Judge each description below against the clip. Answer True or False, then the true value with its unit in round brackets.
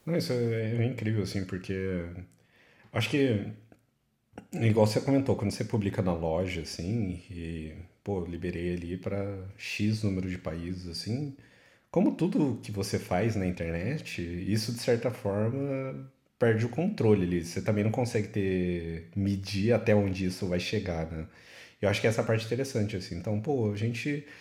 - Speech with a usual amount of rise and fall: True (4.3 semitones)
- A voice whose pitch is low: True (100 Hz)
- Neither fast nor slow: True (165 wpm)